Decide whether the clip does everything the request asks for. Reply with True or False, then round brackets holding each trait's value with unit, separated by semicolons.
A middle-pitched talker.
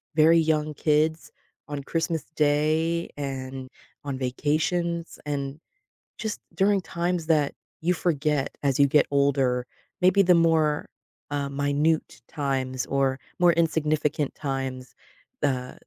True (150 Hz)